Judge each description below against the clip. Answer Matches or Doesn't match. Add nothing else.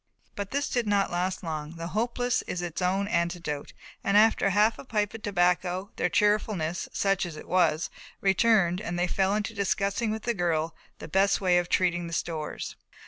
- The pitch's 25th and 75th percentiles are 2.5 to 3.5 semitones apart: Matches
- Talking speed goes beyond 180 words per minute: Matches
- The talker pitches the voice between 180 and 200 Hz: Matches